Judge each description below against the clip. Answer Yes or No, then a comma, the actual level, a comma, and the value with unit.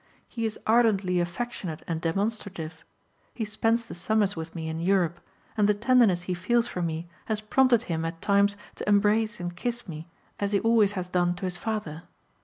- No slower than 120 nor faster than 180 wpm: No, average, 190 wpm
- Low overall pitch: No, high, 200 Hz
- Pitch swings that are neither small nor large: Yes, average, 4.0 semitones